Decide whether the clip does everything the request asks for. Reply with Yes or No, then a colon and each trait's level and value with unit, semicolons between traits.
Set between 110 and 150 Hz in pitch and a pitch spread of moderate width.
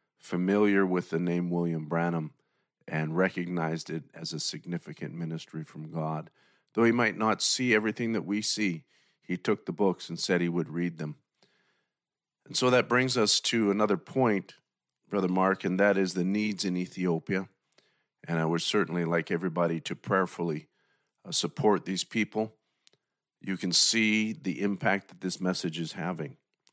No: very low, 95 Hz; average, 3.9 semitones